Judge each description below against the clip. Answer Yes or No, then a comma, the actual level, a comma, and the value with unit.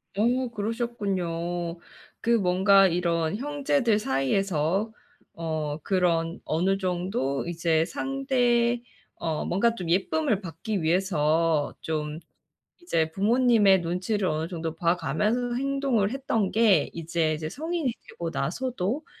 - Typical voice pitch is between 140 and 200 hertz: Yes, high, 190 Hz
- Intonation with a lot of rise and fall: Yes, wide, 6.1 semitones